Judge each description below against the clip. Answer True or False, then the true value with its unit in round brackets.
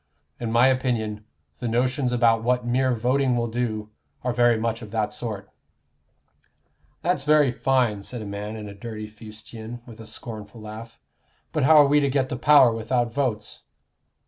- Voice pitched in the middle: False (120 Hz)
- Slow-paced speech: False (170 wpm)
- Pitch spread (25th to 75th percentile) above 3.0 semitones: False (2.7 semitones)